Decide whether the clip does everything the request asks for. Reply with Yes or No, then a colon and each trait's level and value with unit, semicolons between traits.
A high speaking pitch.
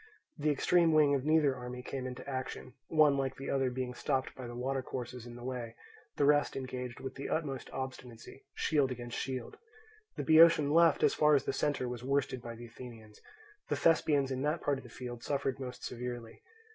No: low, 130 Hz